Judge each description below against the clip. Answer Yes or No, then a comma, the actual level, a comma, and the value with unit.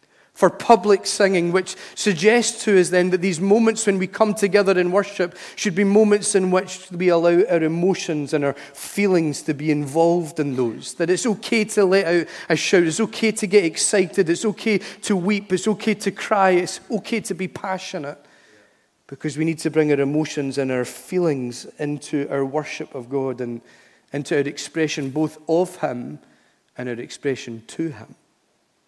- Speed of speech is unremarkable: Yes, average, 180 wpm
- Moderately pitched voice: Yes, medium, 180 Hz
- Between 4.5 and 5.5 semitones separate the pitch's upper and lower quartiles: Yes, average, 5.0 semitones